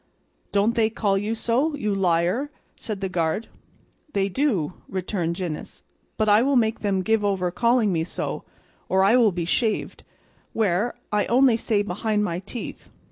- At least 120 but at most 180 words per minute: Yes, average, 165 wpm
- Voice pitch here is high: Yes, high, 205 Hz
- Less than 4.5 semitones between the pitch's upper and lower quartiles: Yes, average, 3.6 semitones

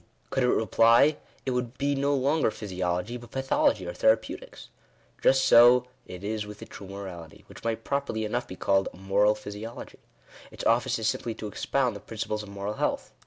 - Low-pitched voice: Yes, low, 115 Hz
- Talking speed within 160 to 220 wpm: Yes, average, 185 wpm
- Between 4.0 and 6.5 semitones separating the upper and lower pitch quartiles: Yes, average, 4.4 semitones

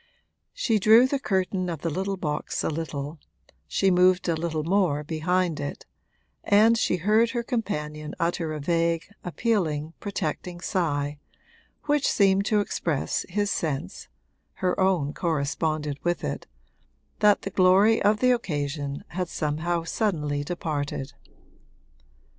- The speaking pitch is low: No, medium, 175 Hz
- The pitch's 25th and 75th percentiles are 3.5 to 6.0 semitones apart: Yes, average, 4.8 semitones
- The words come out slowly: Yes, slow, 130 wpm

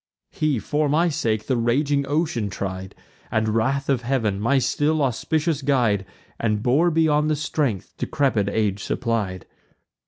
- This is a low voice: Yes, low, 130 Hz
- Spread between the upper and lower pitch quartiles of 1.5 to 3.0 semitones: No, wide, 5.4 semitones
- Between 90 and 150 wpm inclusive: Yes, average, 145 wpm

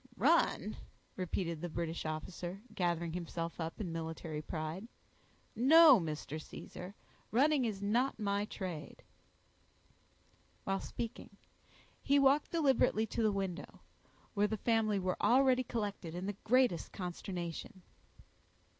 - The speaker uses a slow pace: Yes, slow, 120 wpm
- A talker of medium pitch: No, high, 195 Hz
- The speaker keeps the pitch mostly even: No, average, 5.3 semitones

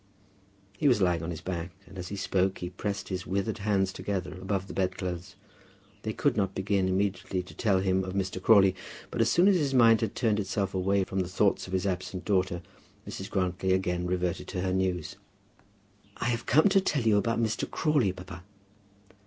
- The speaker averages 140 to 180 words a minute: No, average, 200 wpm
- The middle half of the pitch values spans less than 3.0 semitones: Yes, narrow, 2.4 semitones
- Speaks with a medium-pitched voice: No, very low, 95 Hz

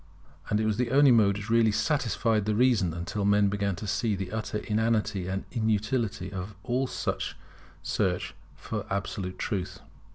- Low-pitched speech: Yes, low, 105 Hz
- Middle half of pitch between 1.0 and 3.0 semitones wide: Yes, narrow, 2.5 semitones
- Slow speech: No, average, 160 wpm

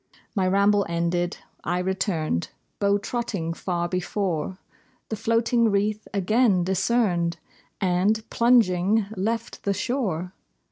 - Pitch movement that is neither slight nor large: Yes, average, 3.7 semitones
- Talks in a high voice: Yes, high, 195 Hz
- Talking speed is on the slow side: Yes, slow, 105 wpm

